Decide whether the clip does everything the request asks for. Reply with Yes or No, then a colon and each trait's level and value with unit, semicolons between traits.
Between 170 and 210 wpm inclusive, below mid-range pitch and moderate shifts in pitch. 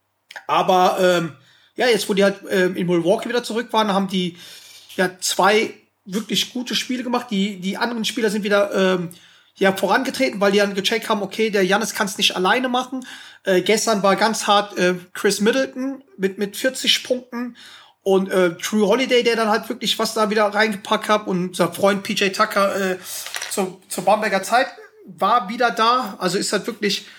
No: fast, 190 wpm; high, 210 Hz; average, 3.2 semitones